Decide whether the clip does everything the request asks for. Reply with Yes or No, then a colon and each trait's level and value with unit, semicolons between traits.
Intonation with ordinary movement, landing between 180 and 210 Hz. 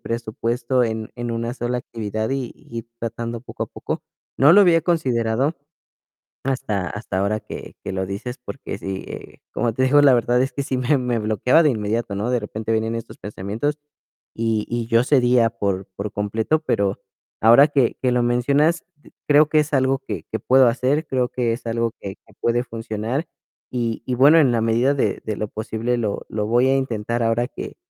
No: average, 3.0 semitones; low, 120 Hz